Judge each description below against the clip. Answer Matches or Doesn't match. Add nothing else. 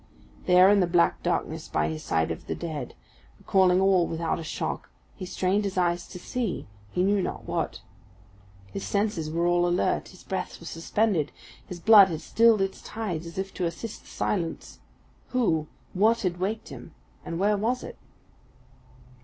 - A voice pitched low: Doesn't match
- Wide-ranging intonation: Doesn't match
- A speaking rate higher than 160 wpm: Matches